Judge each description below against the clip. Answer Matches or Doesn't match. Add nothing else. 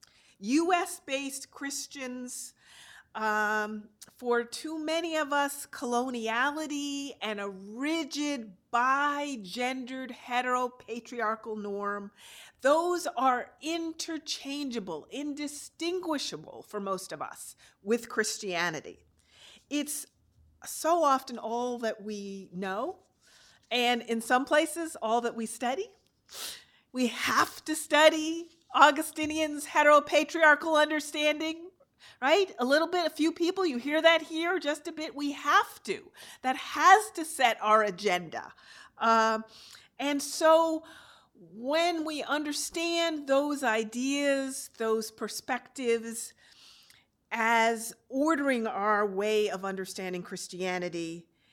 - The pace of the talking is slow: Matches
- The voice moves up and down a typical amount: Doesn't match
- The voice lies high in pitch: Matches